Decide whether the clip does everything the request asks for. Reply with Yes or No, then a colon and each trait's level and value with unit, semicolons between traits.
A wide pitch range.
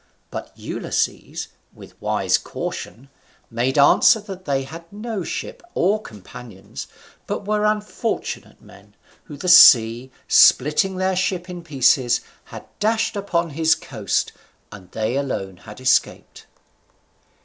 Yes: wide, 7.7 semitones